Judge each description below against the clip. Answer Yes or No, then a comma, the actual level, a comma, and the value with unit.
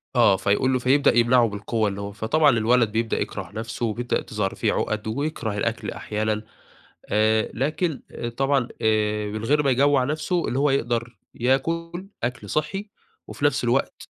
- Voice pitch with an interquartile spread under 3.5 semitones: No, average, 4.3 semitones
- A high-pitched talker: No, low, 120 Hz